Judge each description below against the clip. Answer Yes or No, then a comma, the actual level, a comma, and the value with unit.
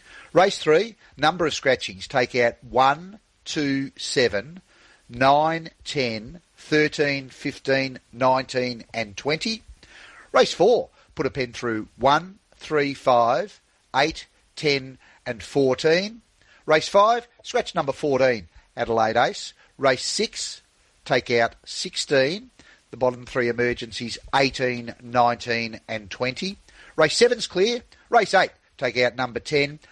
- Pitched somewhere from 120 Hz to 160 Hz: Yes, low, 135 Hz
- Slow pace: Yes, slow, 120 wpm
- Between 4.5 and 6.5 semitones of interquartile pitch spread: Yes, average, 5.2 semitones